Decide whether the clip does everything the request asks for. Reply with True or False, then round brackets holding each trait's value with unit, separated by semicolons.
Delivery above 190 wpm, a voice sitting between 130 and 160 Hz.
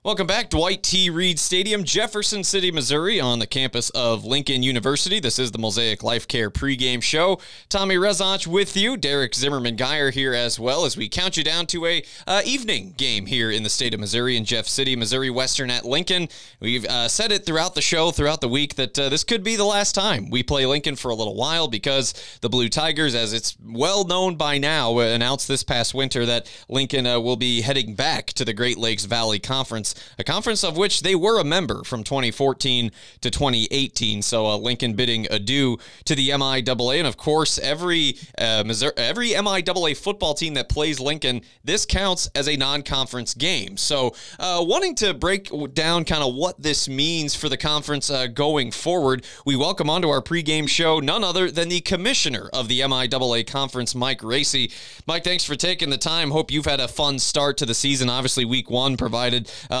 True (205 wpm; 135 Hz)